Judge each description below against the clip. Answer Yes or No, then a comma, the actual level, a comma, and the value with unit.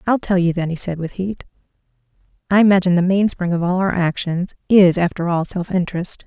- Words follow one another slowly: No, average, 200 wpm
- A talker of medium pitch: Yes, medium, 180 Hz